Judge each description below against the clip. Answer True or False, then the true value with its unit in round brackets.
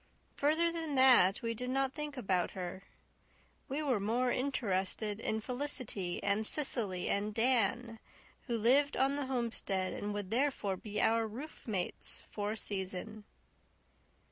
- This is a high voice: True (230 Hz)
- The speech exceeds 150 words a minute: False (140 wpm)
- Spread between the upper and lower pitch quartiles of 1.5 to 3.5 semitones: False (4.6 semitones)